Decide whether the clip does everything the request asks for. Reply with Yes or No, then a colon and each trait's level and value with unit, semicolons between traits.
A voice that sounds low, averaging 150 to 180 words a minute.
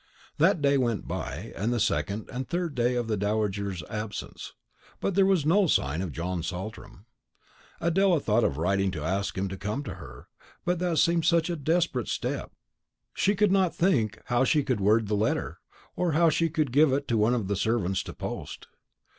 No: low, 120 Hz; average, 195 wpm